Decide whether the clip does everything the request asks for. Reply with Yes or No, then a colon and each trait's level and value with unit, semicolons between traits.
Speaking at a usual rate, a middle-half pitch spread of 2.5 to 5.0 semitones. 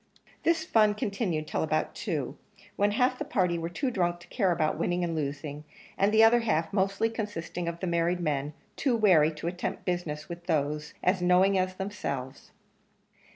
Yes: average, 180 wpm; average, 4.6 semitones